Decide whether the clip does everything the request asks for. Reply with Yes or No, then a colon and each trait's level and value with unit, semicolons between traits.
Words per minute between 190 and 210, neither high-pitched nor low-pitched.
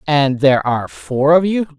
Yes: average, 200 wpm; medium, 145 Hz